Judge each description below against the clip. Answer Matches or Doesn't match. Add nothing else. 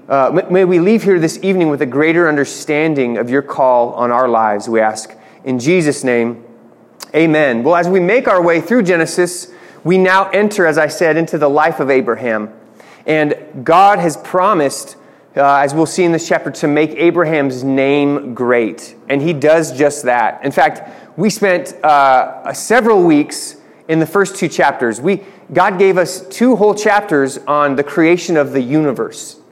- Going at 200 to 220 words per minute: Doesn't match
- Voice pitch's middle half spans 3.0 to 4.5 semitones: Doesn't match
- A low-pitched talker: Doesn't match